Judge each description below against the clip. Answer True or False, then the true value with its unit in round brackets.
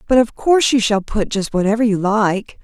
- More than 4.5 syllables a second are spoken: True (5.3 syllables/s)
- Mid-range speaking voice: False (220 Hz)